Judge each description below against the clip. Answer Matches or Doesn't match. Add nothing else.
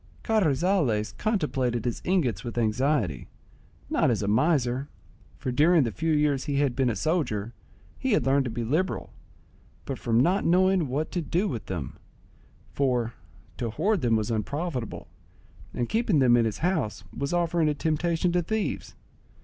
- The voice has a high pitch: Doesn't match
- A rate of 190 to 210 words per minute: Doesn't match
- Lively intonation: Matches